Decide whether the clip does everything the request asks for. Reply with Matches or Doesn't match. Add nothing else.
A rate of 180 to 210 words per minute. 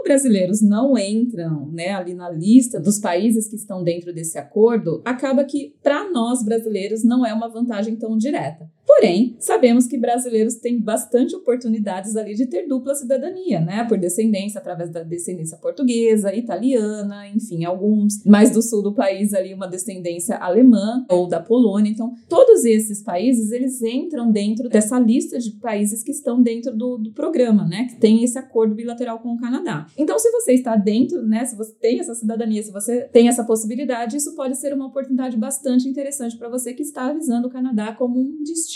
Matches